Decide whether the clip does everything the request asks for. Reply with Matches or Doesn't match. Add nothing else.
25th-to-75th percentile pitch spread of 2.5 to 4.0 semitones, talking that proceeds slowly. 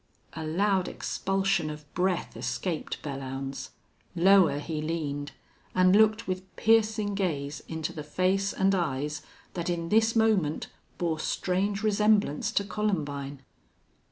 Doesn't match